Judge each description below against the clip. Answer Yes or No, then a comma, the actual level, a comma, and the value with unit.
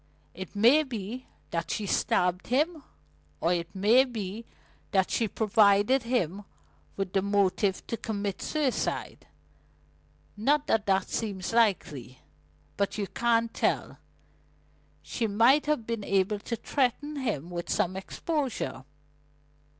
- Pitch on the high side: Yes, high, 210 Hz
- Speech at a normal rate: No, slow, 125 wpm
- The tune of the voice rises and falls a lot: No, average, 4.1 semitones